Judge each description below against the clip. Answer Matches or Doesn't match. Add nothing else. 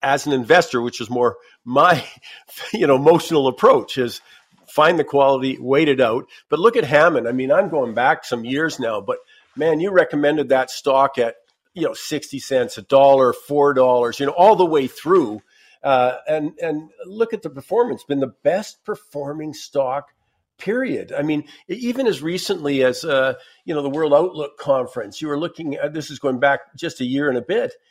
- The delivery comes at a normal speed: Matches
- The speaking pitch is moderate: Matches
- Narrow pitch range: Doesn't match